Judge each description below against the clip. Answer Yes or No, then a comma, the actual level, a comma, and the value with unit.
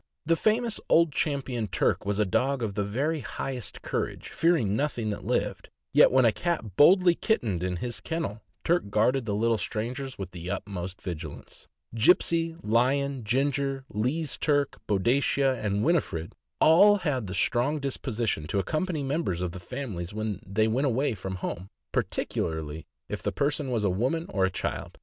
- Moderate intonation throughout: No, wide, 6.3 semitones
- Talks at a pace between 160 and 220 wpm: Yes, average, 170 wpm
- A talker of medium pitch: No, low, 120 Hz